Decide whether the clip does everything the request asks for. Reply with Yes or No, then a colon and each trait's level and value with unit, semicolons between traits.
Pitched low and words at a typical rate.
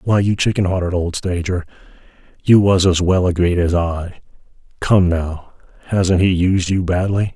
Yes: very low, 90 Hz; average, 165 wpm